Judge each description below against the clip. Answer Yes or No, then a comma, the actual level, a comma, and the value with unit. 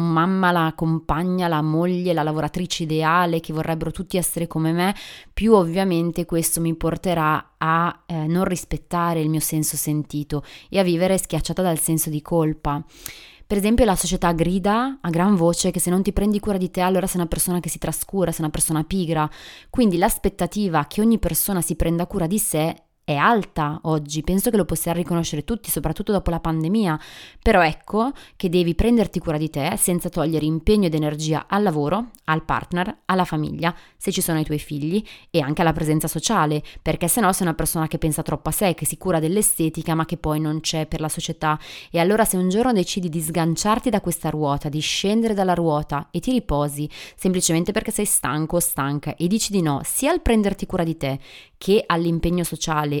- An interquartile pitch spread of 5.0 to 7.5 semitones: No, average, 3.0 semitones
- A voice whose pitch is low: No, medium, 170 Hz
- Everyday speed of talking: No, fast, 200 wpm